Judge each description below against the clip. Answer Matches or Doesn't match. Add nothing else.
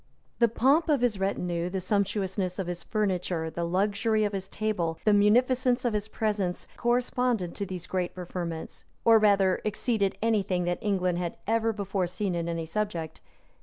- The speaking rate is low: Doesn't match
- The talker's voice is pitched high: Matches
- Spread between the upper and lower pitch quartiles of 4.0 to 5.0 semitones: Doesn't match